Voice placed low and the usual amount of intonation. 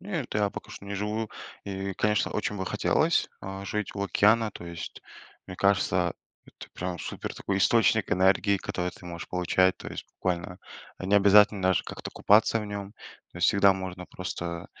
No: low, 100 Hz; narrow, 2.1 semitones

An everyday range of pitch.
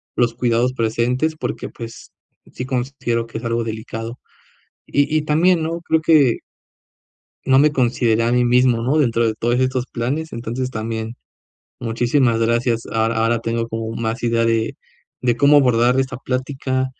No: narrow, 2.2 semitones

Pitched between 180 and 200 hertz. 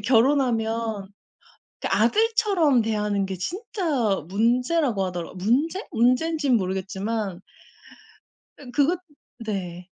No: high, 230 Hz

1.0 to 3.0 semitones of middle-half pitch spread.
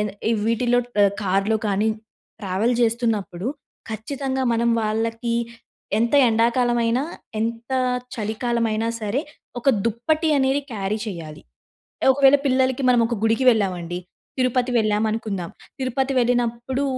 Yes: narrow, 2.6 semitones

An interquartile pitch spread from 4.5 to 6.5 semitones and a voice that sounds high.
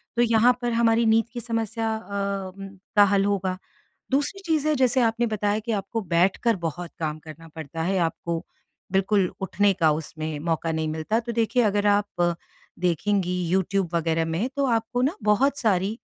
Yes: average, 5.2 semitones; high, 205 Hz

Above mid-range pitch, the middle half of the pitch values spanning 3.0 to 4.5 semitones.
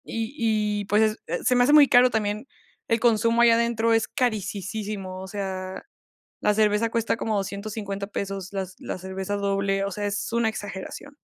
No: high, 210 Hz; narrow, 2.6 semitones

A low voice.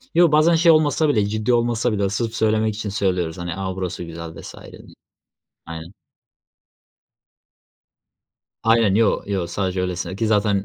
Yes: low, 105 Hz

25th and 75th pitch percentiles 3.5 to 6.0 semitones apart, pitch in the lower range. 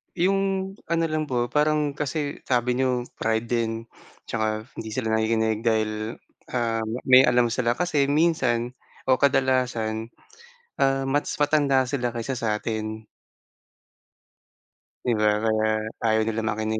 Yes: average, 3.8 semitones; low, 120 Hz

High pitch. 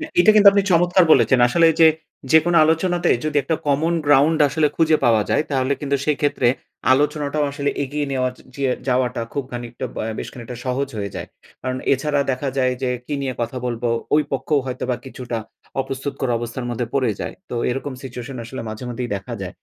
No: low, 135 Hz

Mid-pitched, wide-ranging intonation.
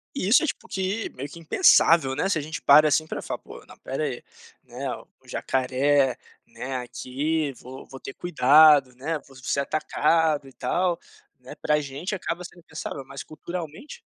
No: medium, 150 Hz; average, 3.8 semitones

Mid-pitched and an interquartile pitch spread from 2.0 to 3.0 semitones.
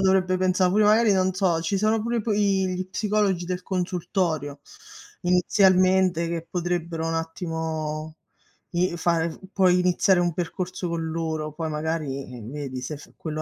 Yes: medium, 175 Hz; narrow, 2.6 semitones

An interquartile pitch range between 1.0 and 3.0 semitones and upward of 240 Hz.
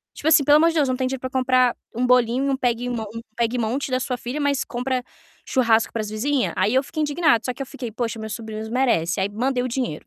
Yes: average, 2.7 semitones; very high, 250 Hz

